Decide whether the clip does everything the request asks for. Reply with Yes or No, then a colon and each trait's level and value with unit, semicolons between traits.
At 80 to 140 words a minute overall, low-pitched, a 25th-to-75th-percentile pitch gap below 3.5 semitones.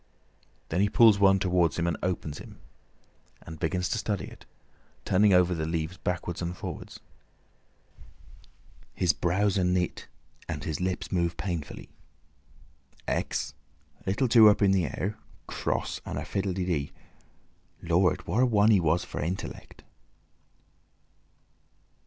Yes: slow, 135 wpm; very low, 90 Hz; average, 2.7 semitones